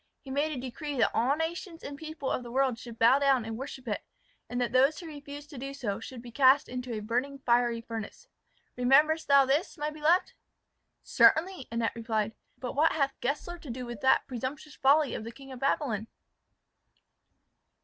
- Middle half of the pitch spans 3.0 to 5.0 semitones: Yes, average, 3.6 semitones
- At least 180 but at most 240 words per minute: Yes, average, 190 wpm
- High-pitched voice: Yes, very high, 270 Hz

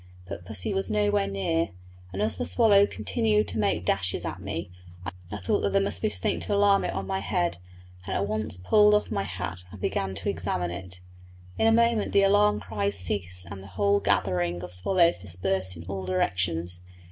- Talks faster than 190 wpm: Yes, average, 200 wpm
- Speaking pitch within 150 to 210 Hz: No, very low, 95 Hz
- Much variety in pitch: No, average, 2.8 semitones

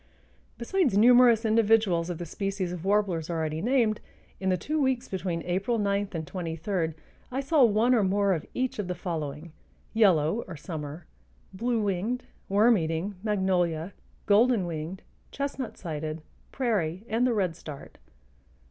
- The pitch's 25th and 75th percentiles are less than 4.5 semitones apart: No, average, 5.2 semitones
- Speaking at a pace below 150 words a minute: Yes, average, 140 wpm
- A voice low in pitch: No, high, 195 Hz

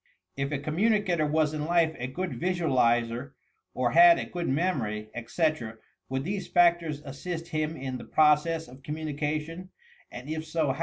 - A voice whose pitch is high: No, medium, 155 Hz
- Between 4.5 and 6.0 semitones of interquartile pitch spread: No, average, 4.1 semitones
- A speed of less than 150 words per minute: No, average, 160 wpm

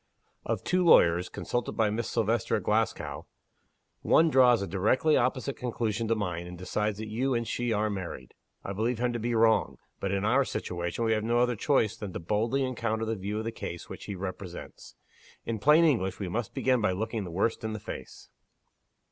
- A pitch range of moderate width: Yes, average, 3.5 semitones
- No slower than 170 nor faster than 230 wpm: Yes, fast, 205 wpm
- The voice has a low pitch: Yes, low, 110 Hz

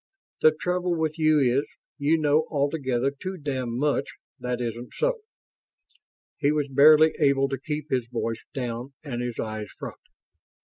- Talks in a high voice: No, medium, 140 Hz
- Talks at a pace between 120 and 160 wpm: Yes, average, 150 wpm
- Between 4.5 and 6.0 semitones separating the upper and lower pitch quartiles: No, average, 3.8 semitones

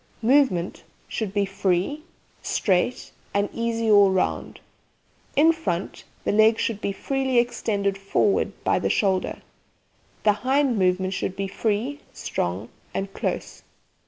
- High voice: Yes, high, 205 Hz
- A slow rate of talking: Yes, slow, 130 wpm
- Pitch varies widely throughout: No, average, 3.9 semitones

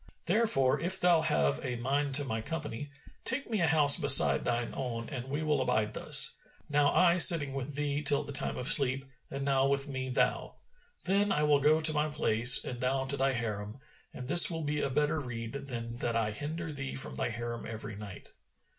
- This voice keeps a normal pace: No, fast, 210 wpm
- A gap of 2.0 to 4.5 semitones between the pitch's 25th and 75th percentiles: Yes, average, 3.6 semitones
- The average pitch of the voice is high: No, low, 135 Hz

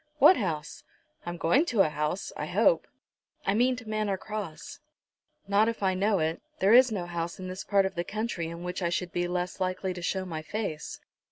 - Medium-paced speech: No, fast, 210 wpm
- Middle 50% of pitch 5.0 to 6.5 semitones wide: No, average, 3.7 semitones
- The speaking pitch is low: No, medium, 185 Hz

